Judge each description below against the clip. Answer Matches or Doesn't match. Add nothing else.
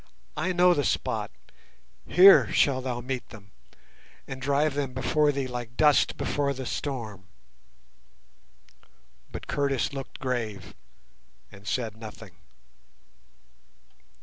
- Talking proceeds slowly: Matches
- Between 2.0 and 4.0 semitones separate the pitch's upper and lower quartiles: Matches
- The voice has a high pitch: Doesn't match